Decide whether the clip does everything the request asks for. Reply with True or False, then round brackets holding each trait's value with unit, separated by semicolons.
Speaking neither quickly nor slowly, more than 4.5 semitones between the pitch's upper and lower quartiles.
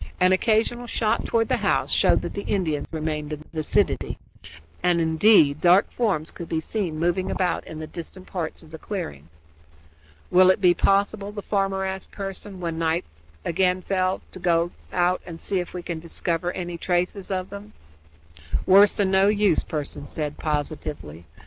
False (175 wpm; 3.3 semitones)